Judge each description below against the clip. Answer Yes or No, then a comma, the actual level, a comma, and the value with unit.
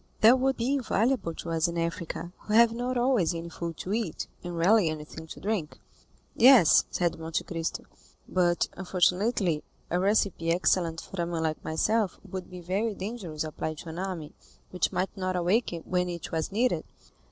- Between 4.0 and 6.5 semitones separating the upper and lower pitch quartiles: Yes, average, 4.5 semitones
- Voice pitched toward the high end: No, medium, 180 Hz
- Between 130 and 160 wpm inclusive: No, average, 175 wpm